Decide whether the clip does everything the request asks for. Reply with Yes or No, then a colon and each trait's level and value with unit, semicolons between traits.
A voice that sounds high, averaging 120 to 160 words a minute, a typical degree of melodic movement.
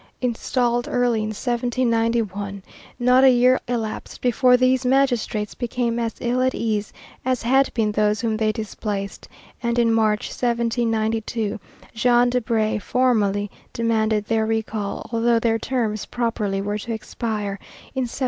No: high, 230 Hz; average, 140 wpm; narrow, 2.3 semitones